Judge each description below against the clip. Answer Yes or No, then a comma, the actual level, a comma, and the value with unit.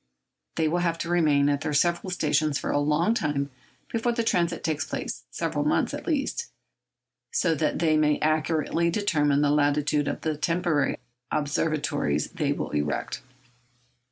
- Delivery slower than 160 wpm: Yes, average, 150 wpm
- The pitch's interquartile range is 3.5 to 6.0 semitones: No, average, 2.8 semitones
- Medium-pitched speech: Yes, medium, 155 Hz